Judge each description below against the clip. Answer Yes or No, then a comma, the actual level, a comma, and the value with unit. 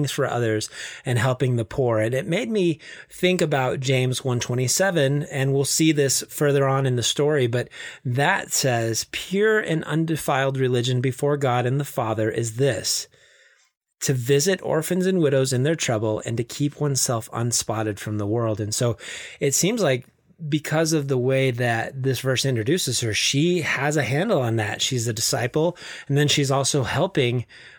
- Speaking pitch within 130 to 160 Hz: Yes, low, 135 Hz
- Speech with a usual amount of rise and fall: Yes, average, 3.5 semitones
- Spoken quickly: No, average, 175 wpm